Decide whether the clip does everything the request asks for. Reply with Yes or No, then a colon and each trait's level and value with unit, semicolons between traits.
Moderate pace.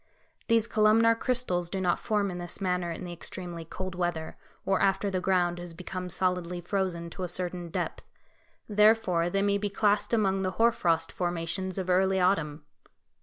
Yes: average, 175 wpm